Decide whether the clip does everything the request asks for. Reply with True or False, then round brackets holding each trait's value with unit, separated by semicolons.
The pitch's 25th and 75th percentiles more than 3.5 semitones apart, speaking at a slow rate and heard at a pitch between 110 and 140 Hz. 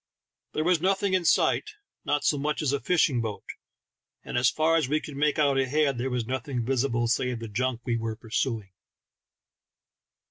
False (4.3 semitones; 180 wpm; 135 Hz)